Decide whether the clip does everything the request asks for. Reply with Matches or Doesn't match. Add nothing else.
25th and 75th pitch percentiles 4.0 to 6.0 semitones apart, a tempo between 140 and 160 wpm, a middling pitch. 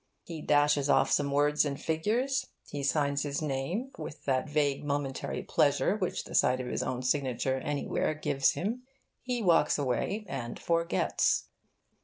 Doesn't match